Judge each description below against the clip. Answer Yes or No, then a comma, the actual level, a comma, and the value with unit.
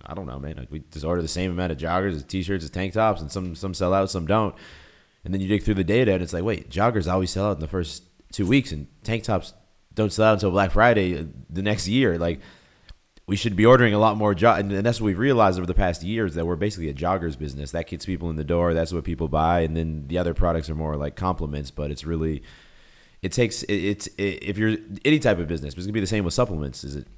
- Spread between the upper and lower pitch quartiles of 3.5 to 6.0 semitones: Yes, average, 4.1 semitones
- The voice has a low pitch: Yes, very low, 90 Hz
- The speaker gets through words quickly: Yes, fast, 280 wpm